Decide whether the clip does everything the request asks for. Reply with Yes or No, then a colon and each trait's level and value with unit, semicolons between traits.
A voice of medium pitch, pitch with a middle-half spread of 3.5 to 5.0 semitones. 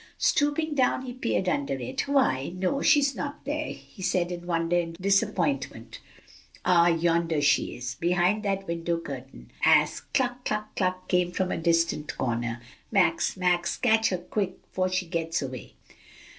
Yes: medium, 180 Hz; average, 4.4 semitones